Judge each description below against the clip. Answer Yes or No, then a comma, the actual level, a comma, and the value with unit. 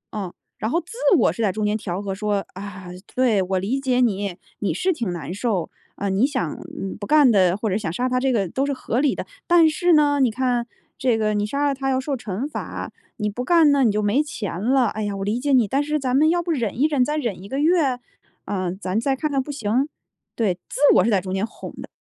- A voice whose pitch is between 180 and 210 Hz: No, high, 235 Hz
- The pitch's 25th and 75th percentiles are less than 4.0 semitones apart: No, wide, 5.5 semitones